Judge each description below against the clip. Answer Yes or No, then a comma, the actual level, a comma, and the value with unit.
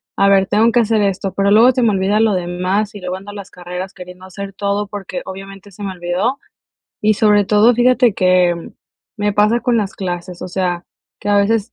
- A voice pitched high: Yes, high, 200 Hz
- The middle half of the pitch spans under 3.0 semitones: Yes, narrow, 2.4 semitones